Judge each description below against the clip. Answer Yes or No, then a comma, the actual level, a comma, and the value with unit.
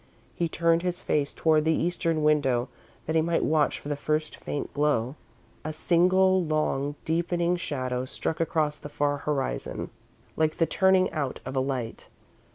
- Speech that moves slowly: No, average, 165 wpm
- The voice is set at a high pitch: No, medium, 155 Hz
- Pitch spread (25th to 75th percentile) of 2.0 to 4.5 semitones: Yes, average, 2.7 semitones